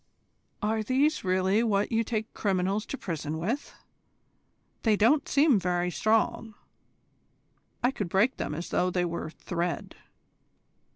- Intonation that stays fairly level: No, average, 4.2 semitones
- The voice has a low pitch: No, high, 205 Hz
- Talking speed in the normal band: No, slow, 130 wpm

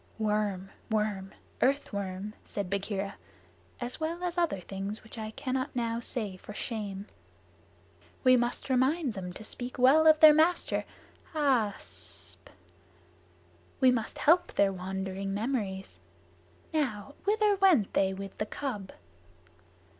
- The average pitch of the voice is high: Yes, high, 220 Hz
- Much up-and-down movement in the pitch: Yes, wide, 5.7 semitones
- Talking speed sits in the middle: No, slow, 130 wpm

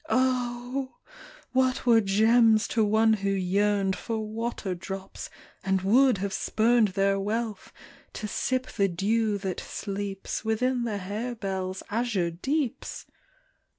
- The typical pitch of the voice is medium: No, high, 215 Hz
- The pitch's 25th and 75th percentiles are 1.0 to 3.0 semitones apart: No, average, 3.5 semitones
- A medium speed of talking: No, slow, 120 wpm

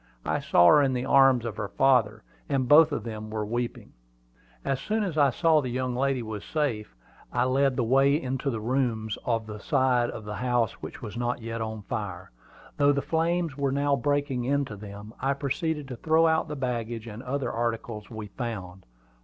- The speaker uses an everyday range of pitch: Yes, average, 4.1 semitones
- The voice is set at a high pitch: No, low, 125 Hz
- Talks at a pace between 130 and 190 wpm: No, fast, 205 wpm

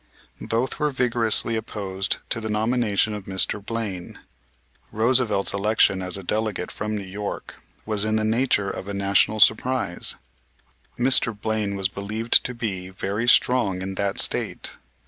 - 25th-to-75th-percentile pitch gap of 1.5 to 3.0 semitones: Yes, average, 2.7 semitones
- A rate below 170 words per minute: Yes, average, 145 wpm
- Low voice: Yes, low, 105 Hz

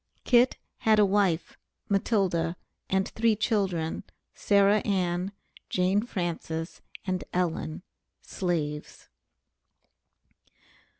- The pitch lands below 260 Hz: Yes, medium, 185 Hz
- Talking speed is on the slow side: Yes, slow, 80 wpm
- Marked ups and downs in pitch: No, average, 3.1 semitones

